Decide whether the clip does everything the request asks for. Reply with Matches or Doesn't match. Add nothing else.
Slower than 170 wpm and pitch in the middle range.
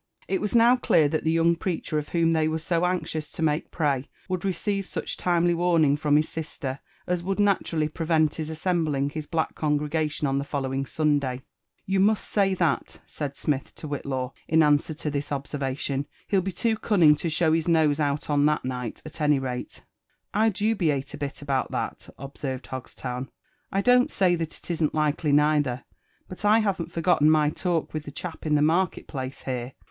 Doesn't match